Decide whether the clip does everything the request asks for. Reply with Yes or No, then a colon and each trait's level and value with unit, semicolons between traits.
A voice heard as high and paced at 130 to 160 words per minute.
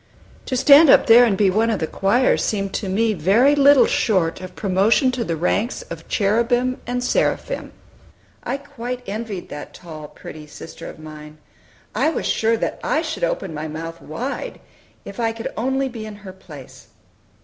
No: high, 215 Hz; average, 180 wpm